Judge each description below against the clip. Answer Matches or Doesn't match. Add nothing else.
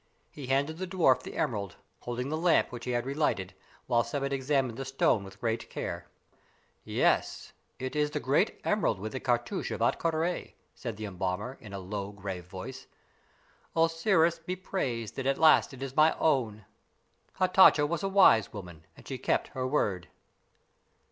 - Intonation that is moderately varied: Doesn't match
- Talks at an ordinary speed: Matches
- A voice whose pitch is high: Doesn't match